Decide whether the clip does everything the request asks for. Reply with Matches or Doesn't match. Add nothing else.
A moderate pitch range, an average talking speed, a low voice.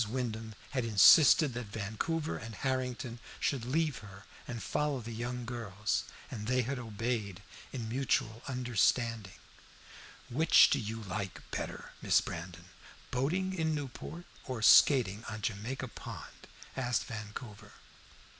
Doesn't match